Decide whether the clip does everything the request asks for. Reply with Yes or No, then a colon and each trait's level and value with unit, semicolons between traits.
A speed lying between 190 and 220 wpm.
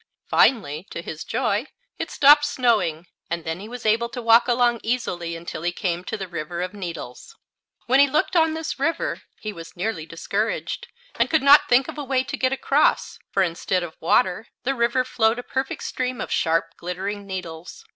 Yes: average, 195 wpm